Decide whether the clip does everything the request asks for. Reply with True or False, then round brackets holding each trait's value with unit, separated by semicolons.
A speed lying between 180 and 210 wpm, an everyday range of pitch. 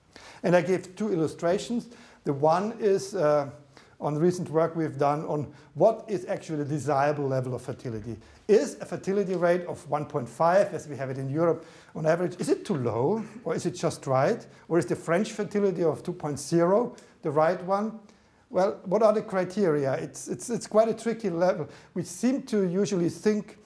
True (185 wpm; 5.0 semitones)